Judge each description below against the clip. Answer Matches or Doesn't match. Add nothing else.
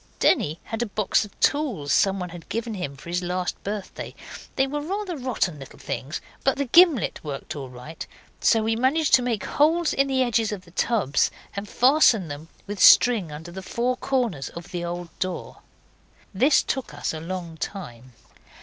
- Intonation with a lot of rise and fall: Matches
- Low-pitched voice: Doesn't match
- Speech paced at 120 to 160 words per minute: Doesn't match